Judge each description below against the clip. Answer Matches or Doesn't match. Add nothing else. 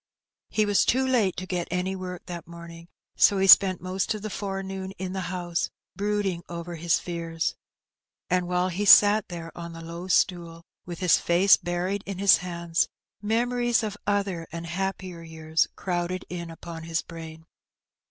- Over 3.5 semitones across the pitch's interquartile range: Doesn't match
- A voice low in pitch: Doesn't match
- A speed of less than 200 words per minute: Matches